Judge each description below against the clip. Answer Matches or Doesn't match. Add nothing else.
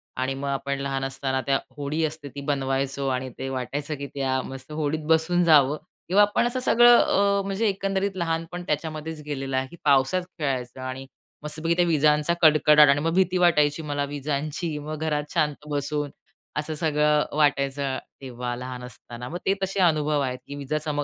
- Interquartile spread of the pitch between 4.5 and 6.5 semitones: Doesn't match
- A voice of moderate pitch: Matches